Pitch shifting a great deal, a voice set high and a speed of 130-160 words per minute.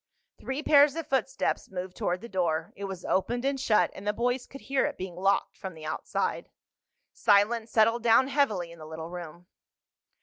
No: wide, 6.4 semitones; high, 210 Hz; average, 190 wpm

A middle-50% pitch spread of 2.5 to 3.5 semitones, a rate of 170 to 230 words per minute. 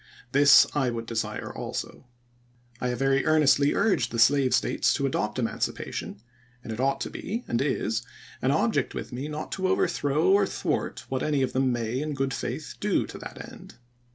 Yes: average, 3.1 semitones; average, 190 wpm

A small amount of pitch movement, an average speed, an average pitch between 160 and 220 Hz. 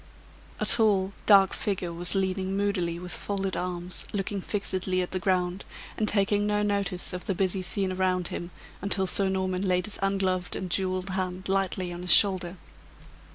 Yes: narrow, 1.4 semitones; average, 170 wpm; high, 190 Hz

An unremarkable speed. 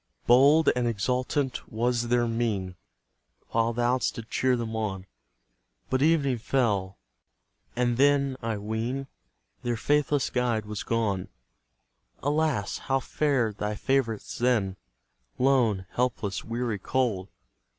No: slow, 115 wpm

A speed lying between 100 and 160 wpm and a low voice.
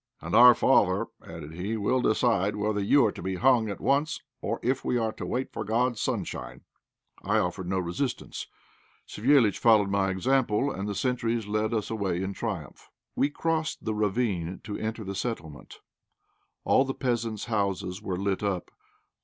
No: average, 170 wpm; low, 110 Hz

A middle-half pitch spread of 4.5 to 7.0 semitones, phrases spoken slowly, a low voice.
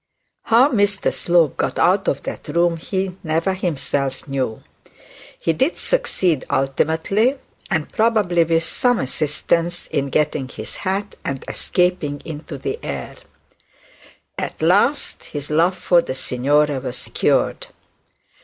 No: average, 4.8 semitones; slow, 130 wpm; medium, 165 Hz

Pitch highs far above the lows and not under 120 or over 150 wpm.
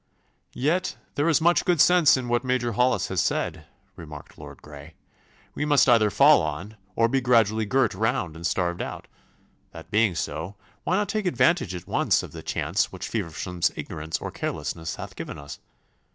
No: wide, 8.4 semitones; average, 180 wpm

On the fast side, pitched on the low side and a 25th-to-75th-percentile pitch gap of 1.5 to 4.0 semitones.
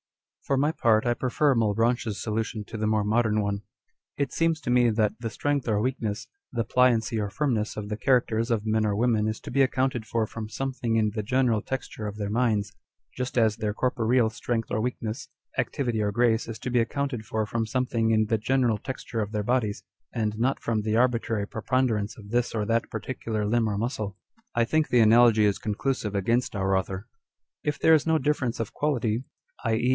Yes: fast, 210 wpm; low, 115 Hz; narrow, 2.6 semitones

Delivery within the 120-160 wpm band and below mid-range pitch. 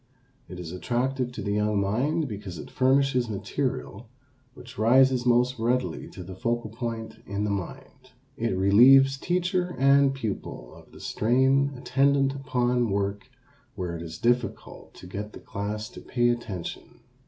Yes: average, 155 wpm; low, 120 Hz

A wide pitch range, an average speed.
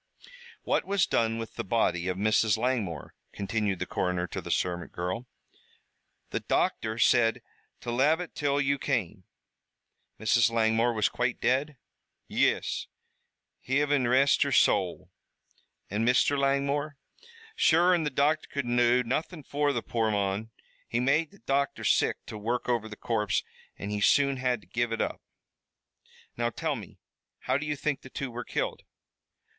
No: average, 4.2 semitones; average, 160 wpm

